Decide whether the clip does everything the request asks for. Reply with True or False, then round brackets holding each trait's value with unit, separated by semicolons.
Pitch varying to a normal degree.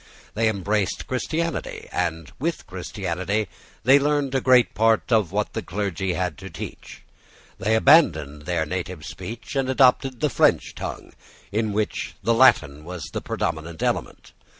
False (6.6 semitones)